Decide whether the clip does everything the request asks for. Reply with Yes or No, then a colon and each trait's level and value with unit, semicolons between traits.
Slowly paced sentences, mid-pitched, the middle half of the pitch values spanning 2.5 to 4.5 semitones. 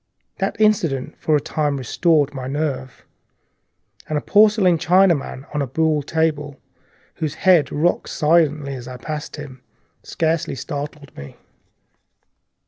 Yes: slow, 125 wpm; medium, 150 Hz; average, 2.9 semitones